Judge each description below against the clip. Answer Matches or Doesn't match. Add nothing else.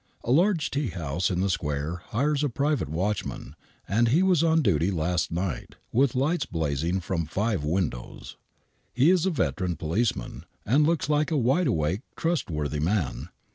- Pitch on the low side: Matches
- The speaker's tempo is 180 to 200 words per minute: Doesn't match